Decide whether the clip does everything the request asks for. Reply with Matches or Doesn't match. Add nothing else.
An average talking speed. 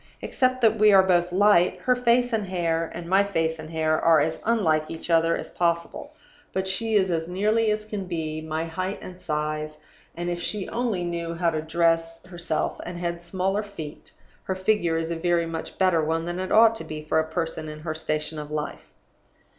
Doesn't match